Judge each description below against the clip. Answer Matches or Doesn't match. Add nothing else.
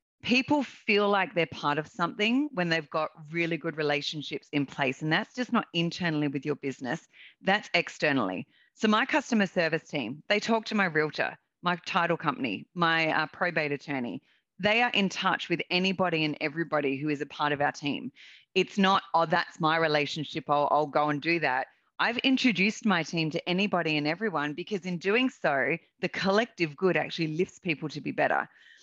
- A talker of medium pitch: Matches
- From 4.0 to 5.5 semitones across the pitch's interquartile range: Matches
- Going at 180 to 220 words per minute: Matches